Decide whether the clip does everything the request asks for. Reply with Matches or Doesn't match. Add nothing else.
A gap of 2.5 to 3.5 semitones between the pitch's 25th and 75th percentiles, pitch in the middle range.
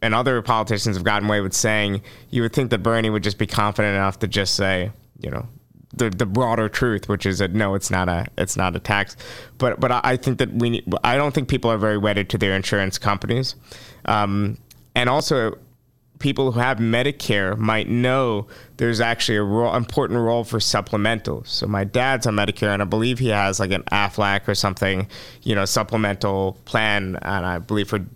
Doesn't match